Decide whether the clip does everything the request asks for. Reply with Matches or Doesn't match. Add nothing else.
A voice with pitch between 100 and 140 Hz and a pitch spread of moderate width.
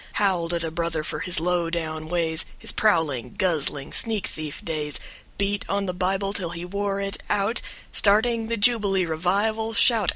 Doesn't match